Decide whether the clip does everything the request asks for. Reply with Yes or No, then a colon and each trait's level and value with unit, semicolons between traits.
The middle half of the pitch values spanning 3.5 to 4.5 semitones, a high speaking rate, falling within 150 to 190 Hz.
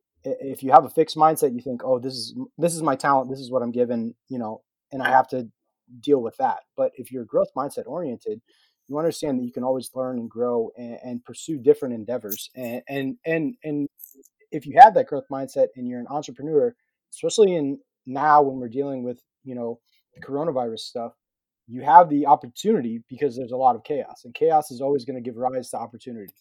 No: average, 4.0 semitones; fast, 215 wpm; low, 135 Hz